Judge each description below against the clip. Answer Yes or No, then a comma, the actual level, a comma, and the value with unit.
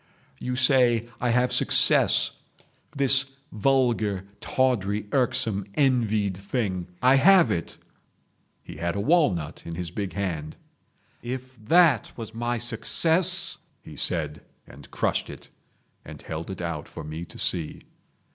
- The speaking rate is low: Yes, slow, 130 wpm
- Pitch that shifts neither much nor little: No, wide, 6.2 semitones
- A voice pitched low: Yes, low, 115 Hz